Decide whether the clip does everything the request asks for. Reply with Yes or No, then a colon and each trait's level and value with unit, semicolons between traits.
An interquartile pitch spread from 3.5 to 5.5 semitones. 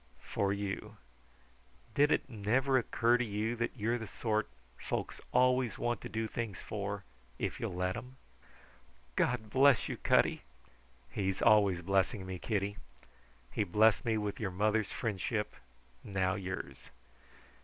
No: average, 3.1 semitones